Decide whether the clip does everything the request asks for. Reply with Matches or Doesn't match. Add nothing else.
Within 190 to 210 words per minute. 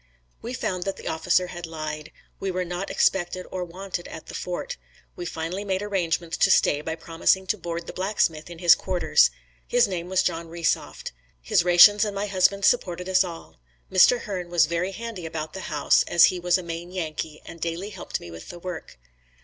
Matches